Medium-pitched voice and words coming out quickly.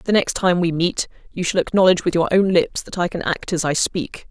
Yes: medium, 180 Hz; fast, 265 wpm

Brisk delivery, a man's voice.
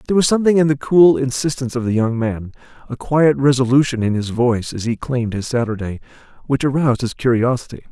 No: average, 195 wpm; male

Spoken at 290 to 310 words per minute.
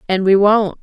No: fast, 215 wpm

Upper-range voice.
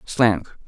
No: low, 110 Hz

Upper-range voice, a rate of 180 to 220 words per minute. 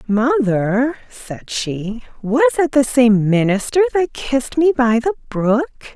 No: very high, 250 Hz; average, 140 wpm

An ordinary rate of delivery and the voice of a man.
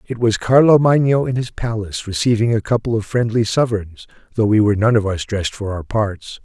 No: fast, 215 wpm; male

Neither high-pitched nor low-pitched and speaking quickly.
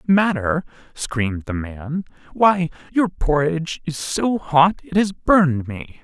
No: medium, 160 Hz; average, 140 wpm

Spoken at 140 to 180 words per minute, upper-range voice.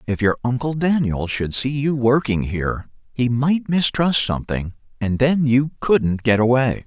No: average, 165 wpm; low, 125 Hz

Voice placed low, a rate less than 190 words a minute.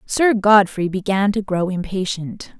No: high, 195 Hz; average, 140 wpm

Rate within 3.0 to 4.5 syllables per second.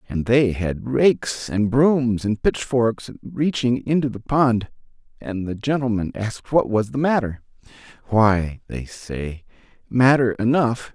Yes: 3.9 syllables/s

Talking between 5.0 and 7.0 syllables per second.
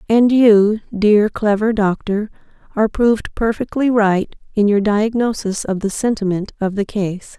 No: 4.4 syllables/s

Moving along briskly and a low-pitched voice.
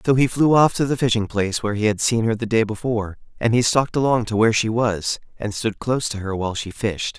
Yes: fast, 265 wpm; low, 110 Hz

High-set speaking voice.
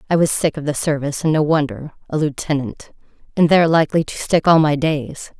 No: medium, 150 Hz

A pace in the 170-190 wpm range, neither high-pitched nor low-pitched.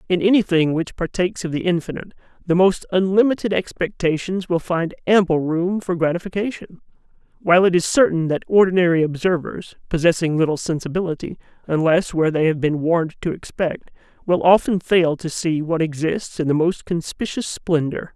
No: average, 155 wpm; medium, 170 Hz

